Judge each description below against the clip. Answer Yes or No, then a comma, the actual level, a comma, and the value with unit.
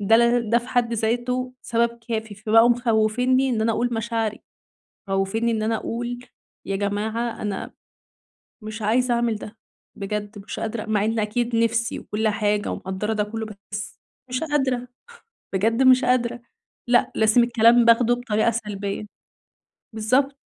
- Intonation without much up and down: Yes, narrow, 2.1 semitones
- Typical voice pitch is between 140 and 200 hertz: No, high, 230 Hz